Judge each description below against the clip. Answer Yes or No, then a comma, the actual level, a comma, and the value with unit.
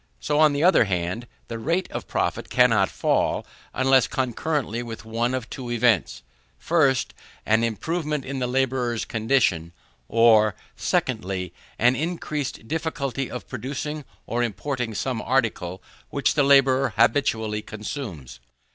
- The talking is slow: Yes, slow, 130 wpm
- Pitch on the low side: Yes, low, 125 Hz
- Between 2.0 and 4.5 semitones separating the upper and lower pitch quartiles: Yes, average, 3.9 semitones